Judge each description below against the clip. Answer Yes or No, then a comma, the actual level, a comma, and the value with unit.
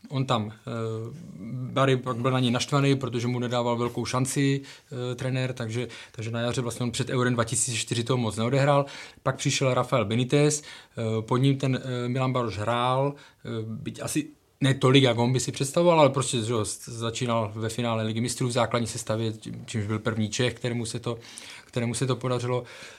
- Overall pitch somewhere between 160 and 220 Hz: No, low, 125 Hz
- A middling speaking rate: No, fast, 185 wpm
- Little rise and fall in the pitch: Yes, narrow, 2.2 semitones